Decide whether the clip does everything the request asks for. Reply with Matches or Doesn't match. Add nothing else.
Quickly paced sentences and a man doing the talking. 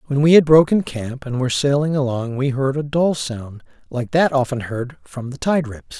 Matches